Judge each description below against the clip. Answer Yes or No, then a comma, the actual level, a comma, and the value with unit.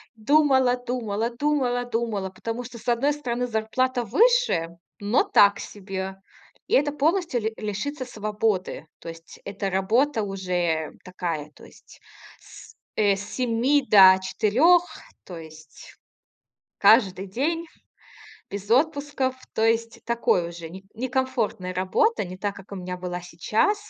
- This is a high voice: Yes, high, 220 Hz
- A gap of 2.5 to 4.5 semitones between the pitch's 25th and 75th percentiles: No, wide, 5.4 semitones